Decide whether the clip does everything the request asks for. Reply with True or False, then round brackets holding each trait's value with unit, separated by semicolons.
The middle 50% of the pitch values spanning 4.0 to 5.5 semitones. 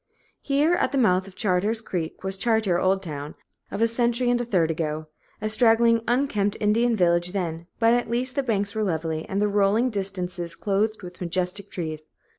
True (4.4 semitones)